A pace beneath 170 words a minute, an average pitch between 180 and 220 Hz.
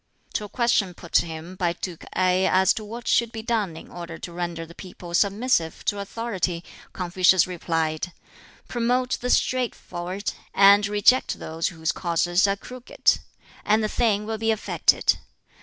Yes: average, 160 wpm; high, 190 Hz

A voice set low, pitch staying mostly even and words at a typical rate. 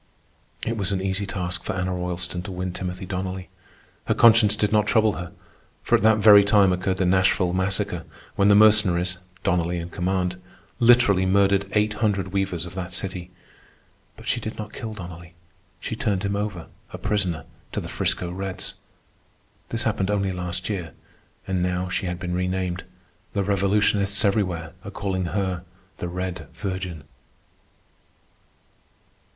Yes: very low, 95 Hz; narrow, 2.1 semitones; average, 155 wpm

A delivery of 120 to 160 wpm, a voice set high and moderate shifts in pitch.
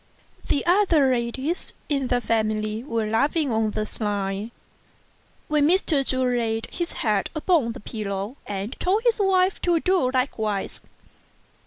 No: average, 140 wpm; very high, 250 Hz; wide, 6.7 semitones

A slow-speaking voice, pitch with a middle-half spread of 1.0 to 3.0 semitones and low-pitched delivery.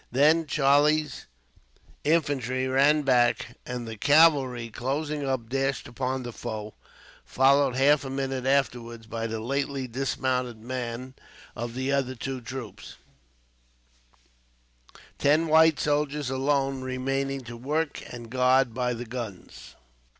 Yes: slow, 120 wpm; narrow, 2.5 semitones; low, 130 Hz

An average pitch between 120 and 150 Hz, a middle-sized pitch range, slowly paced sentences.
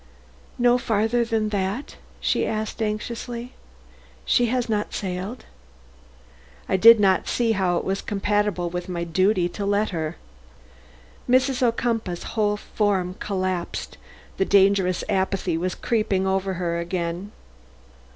No: high, 200 Hz; average, 3.3 semitones; slow, 125 wpm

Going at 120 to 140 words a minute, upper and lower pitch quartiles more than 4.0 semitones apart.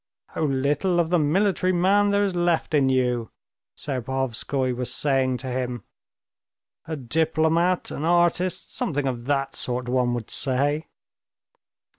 Yes: slow, 135 wpm; average, 5.1 semitones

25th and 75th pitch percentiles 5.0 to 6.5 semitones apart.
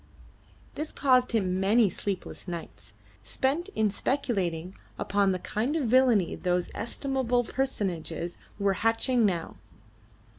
Yes: wide, 5.6 semitones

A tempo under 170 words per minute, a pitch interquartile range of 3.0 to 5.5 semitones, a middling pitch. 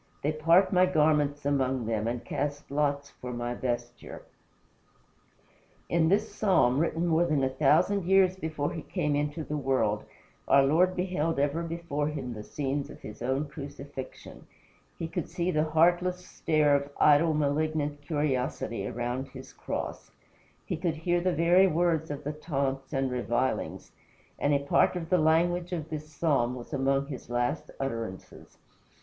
Yes: average, 160 wpm; average, 3.6 semitones; medium, 150 Hz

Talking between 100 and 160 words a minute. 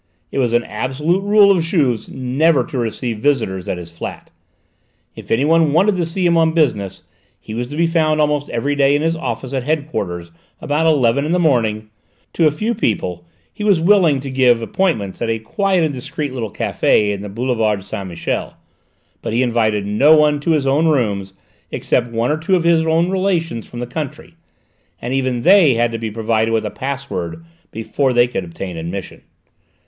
No: average, 195 wpm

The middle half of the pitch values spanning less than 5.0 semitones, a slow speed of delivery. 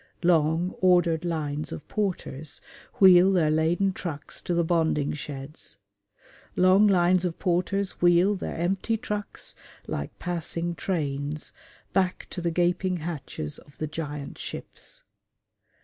Yes: average, 3.1 semitones; slow, 125 wpm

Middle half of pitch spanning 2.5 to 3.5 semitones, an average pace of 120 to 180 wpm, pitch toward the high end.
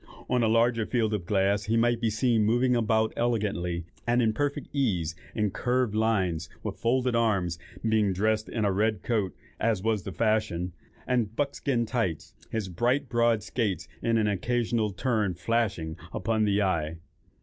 No: average, 3.1 semitones; average, 165 wpm; low, 110 Hz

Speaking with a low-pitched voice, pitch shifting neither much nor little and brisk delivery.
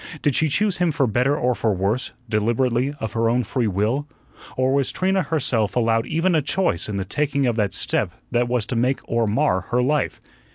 Yes: low, 125 Hz; average, 4.3 semitones; fast, 210 wpm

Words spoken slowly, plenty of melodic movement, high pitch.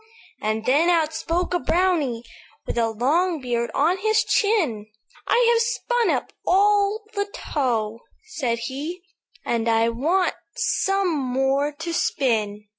Yes: slow, 130 wpm; wide, 8.0 semitones; very high, 310 Hz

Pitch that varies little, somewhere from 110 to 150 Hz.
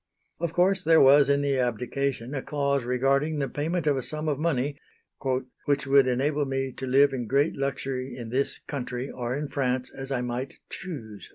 Yes: narrow, 2.3 semitones; low, 135 Hz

